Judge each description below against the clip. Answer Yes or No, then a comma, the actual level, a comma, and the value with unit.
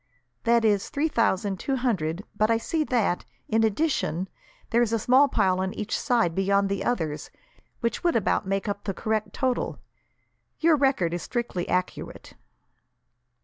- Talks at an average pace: Yes, average, 160 wpm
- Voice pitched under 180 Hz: No, high, 215 Hz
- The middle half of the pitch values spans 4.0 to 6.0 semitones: Yes, average, 4.3 semitones